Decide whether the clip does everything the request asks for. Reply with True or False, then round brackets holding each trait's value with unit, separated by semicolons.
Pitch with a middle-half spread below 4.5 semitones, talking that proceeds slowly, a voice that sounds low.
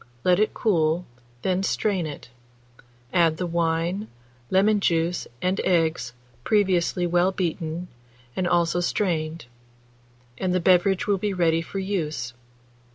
False (2.5 semitones; 125 wpm; 175 Hz)